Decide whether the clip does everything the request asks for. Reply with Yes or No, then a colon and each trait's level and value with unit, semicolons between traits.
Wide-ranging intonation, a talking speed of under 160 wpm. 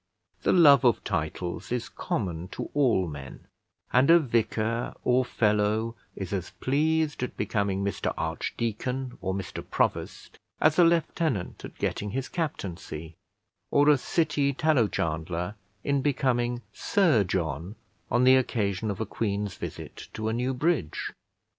Yes: wide, 6.0 semitones; average, 140 wpm